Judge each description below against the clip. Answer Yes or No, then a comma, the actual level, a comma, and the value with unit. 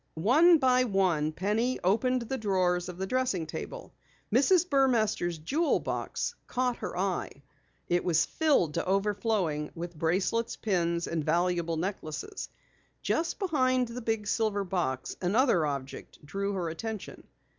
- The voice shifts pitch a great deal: Yes, wide, 6.5 semitones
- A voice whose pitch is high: Yes, high, 195 Hz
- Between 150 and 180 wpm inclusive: No, slow, 135 wpm